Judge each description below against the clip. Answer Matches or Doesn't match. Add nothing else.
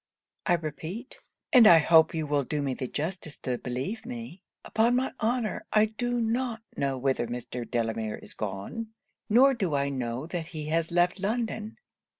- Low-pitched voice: Doesn't match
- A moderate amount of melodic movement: Doesn't match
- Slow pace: Doesn't match